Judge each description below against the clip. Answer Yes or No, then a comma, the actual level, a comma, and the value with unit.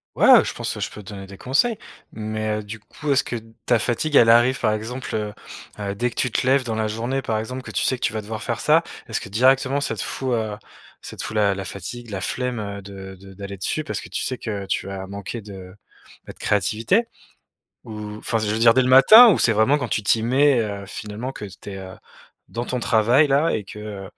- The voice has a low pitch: Yes, low, 110 Hz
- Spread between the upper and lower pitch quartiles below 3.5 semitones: No, average, 3.8 semitones